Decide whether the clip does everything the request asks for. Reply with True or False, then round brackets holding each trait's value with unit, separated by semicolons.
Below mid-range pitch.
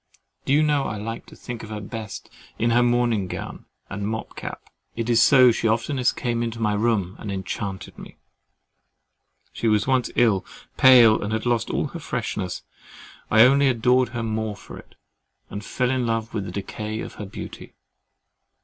True (115 Hz)